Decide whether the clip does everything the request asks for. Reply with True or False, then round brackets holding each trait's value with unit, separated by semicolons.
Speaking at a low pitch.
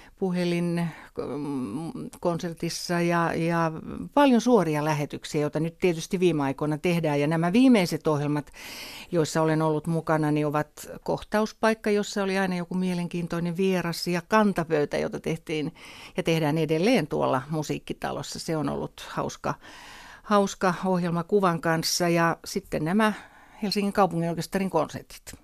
False (170 Hz)